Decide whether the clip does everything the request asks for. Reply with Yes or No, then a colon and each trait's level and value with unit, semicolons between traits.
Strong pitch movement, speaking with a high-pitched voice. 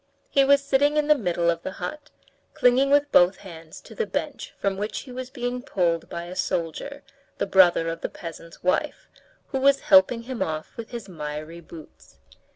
Yes: wide, 8.0 semitones; high, 200 Hz